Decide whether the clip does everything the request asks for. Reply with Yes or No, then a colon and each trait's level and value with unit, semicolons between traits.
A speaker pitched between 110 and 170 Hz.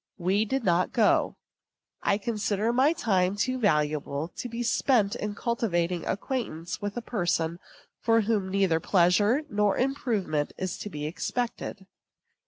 No: high, 205 Hz